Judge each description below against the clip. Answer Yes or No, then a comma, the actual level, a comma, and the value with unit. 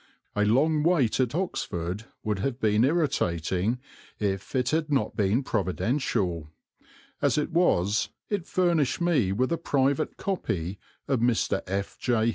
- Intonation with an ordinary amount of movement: No, wide, 7.2 semitones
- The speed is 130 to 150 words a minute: Yes, average, 140 wpm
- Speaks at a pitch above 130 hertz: No, low, 120 Hz